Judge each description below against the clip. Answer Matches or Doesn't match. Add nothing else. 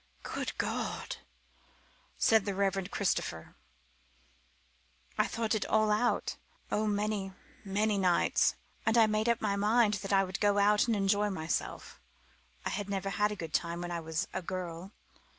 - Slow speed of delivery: Doesn't match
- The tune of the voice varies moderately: Doesn't match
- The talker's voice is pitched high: Matches